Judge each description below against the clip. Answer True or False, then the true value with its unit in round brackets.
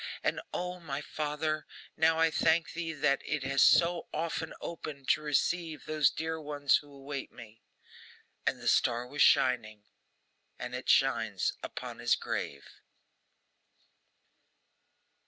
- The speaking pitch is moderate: True (150 Hz)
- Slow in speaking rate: True (130 wpm)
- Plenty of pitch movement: False (3.2 semitones)